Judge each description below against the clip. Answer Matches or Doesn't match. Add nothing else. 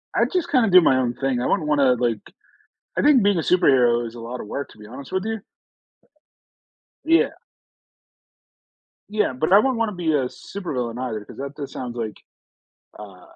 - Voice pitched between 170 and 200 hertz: Doesn't match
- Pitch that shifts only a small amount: Doesn't match